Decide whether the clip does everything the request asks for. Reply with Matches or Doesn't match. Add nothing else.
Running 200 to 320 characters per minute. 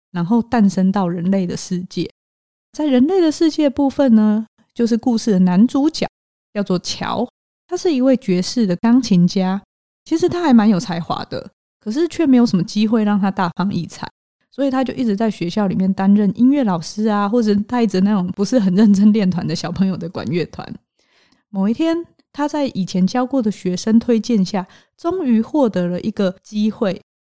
Matches